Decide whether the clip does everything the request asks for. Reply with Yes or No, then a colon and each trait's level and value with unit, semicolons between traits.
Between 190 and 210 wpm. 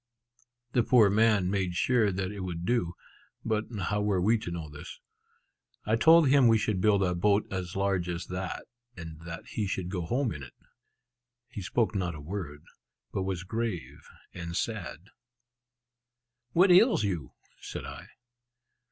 No: average, 160 wpm